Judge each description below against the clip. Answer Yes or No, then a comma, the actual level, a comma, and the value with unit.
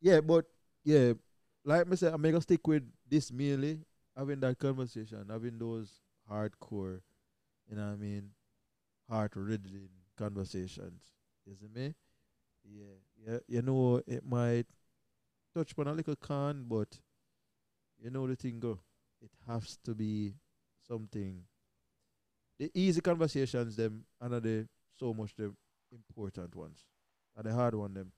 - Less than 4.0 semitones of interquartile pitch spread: No, average, 4.9 semitones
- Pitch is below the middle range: Yes, low, 115 Hz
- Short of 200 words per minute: Yes, average, 145 wpm